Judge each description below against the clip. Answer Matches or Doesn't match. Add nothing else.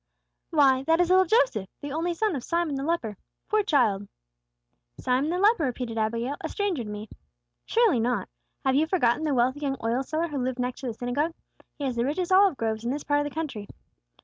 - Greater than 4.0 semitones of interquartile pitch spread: Matches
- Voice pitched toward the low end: Doesn't match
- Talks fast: Matches